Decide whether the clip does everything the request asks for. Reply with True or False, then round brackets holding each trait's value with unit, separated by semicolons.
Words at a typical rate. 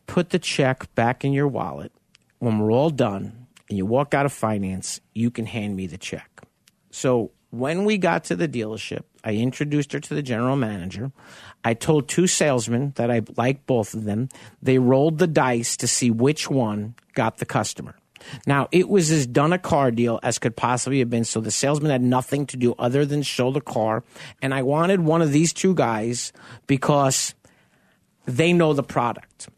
True (195 wpm)